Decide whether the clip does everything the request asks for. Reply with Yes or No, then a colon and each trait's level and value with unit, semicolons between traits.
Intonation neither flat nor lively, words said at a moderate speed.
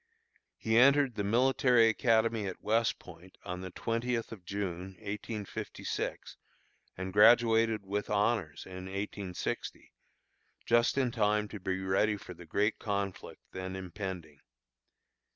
No: average, 3.3 semitones; slow, 125 wpm